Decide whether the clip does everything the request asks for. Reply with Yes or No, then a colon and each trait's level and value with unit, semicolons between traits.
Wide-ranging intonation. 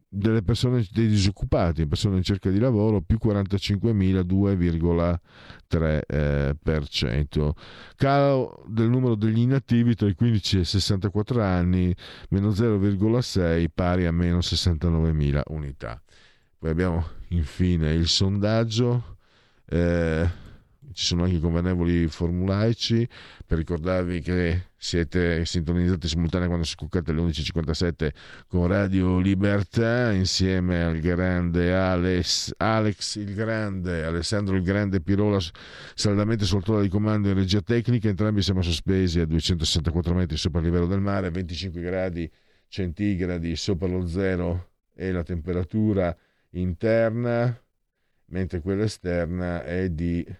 No: average, 3.4 semitones